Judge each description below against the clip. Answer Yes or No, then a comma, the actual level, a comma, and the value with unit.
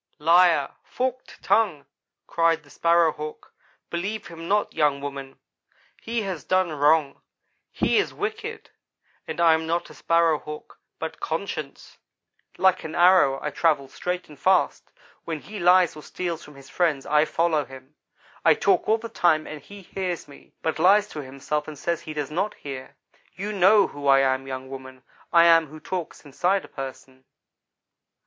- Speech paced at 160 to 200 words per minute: Yes, average, 170 wpm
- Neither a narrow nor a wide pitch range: Yes, average, 4.2 semitones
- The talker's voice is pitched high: No, medium, 160 Hz